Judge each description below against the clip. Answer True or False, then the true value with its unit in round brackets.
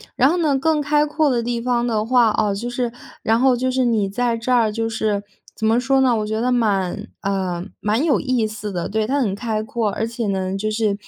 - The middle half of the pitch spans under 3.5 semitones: True (3.0 semitones)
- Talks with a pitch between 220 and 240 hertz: True (230 Hz)